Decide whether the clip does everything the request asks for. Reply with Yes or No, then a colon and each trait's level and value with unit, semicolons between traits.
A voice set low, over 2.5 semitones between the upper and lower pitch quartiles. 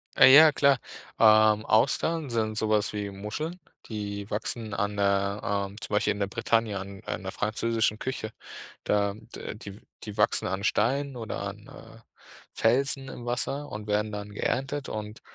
Yes: low, 110 Hz; average, 2.9 semitones